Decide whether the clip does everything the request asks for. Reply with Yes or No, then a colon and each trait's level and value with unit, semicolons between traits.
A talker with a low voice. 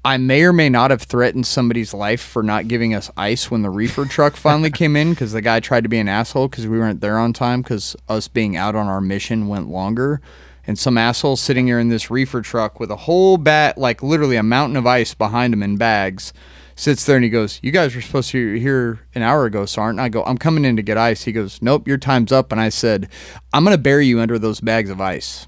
Yes: low, 115 Hz